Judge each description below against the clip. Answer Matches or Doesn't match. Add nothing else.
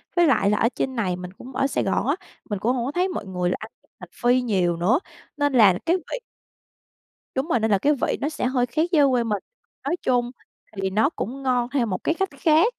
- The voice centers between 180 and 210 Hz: Doesn't match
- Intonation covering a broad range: Matches